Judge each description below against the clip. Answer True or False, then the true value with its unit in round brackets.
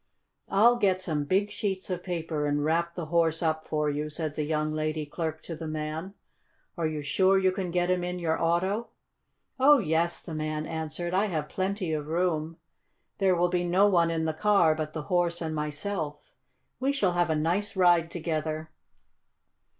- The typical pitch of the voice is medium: True (165 Hz)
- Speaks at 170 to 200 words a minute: True (190 wpm)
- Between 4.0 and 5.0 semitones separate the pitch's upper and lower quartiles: False (2.9 semitones)